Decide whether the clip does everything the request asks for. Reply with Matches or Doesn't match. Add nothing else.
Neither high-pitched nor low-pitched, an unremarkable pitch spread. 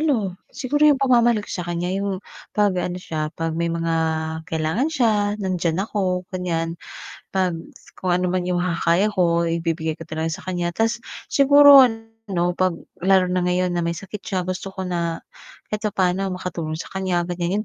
Matches